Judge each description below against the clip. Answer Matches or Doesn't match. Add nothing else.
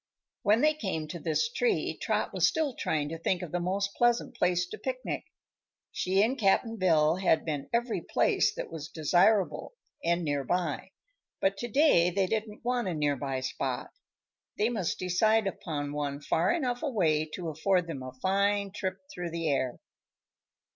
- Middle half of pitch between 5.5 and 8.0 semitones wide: Matches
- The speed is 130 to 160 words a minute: Doesn't match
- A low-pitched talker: Doesn't match